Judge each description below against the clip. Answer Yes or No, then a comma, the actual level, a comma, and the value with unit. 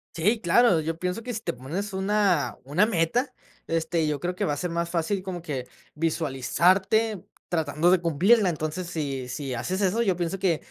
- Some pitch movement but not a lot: Yes, average, 3.7 semitones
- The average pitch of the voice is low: No, medium, 175 Hz